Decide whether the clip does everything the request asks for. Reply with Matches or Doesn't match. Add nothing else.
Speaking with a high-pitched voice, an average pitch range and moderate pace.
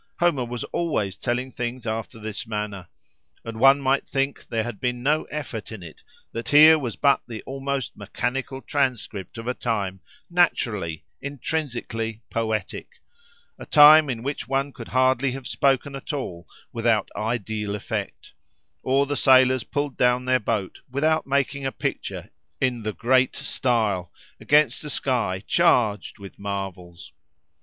Doesn't match